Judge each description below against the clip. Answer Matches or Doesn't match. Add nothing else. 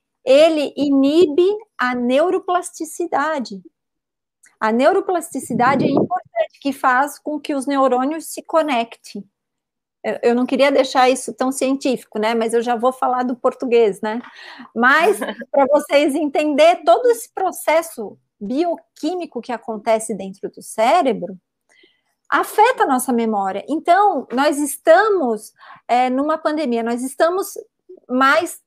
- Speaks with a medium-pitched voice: Doesn't match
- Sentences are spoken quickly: Doesn't match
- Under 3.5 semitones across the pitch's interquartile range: Doesn't match